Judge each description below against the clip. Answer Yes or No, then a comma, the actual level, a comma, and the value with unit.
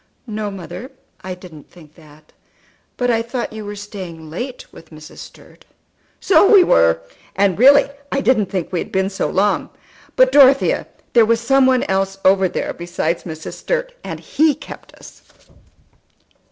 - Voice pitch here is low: No, high, 200 Hz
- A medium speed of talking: Yes, average, 165 wpm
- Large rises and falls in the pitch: Yes, wide, 6.6 semitones